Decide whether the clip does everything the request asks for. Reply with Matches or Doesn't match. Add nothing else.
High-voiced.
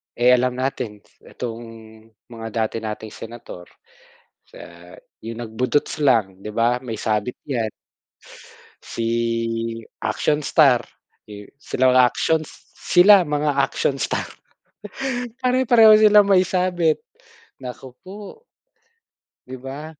Doesn't match